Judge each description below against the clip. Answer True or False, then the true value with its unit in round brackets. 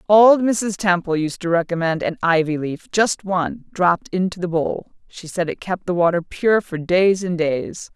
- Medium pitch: True (180 Hz)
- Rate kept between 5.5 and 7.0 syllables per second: False (4.6 syllables/s)